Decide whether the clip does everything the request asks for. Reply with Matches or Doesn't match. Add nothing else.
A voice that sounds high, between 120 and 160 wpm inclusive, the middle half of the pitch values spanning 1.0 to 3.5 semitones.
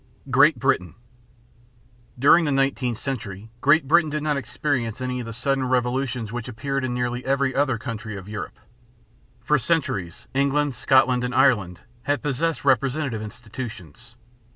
Doesn't match